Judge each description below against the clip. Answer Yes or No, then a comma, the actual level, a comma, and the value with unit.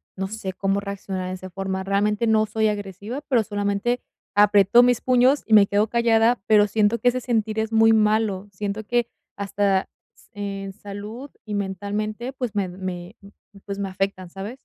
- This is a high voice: Yes, high, 205 Hz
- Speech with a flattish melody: Yes, narrow, 2.2 semitones